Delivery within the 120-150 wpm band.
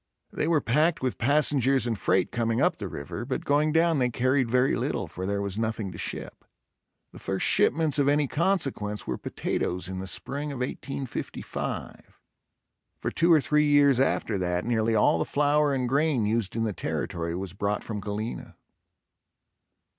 No: average, 175 wpm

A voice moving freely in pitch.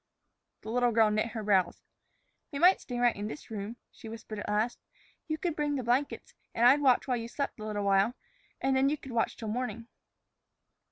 No: average, 3.7 semitones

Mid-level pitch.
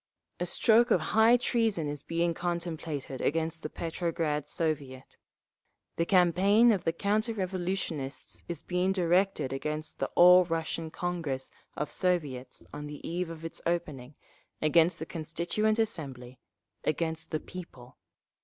Yes: medium, 165 Hz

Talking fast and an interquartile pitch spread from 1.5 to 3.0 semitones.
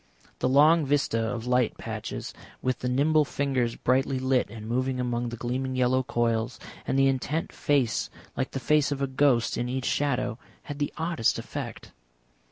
No: average, 175 wpm; narrow, 2.4 semitones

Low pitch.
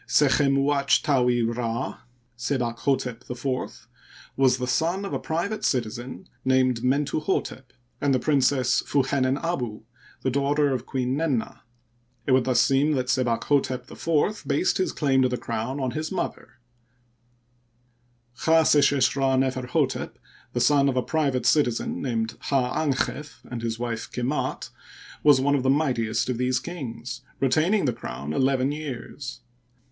Yes: low, 130 Hz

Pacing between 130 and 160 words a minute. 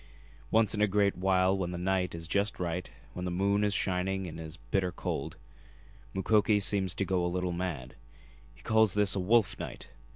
No: average, 200 wpm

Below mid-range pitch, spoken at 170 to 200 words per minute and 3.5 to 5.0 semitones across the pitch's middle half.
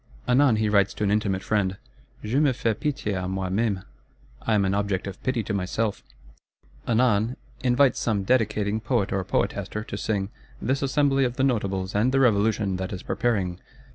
Yes: low, 105 Hz; average, 180 wpm; average, 3.9 semitones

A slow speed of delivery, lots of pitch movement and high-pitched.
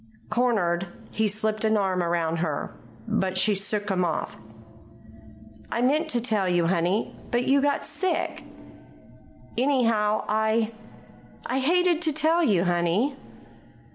Yes: slow, 130 wpm; wide, 5.8 semitones; high, 215 Hz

